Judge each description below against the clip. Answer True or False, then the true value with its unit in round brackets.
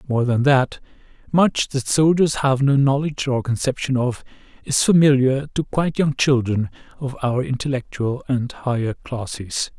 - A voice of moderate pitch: False (130 Hz)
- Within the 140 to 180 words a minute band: True (145 wpm)